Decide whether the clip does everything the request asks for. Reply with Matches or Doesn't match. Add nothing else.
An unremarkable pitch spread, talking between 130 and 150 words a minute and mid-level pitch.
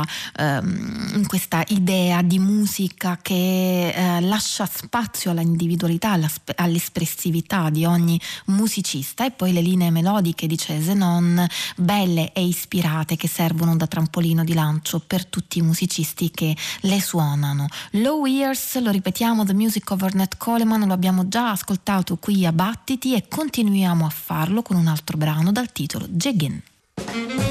Matches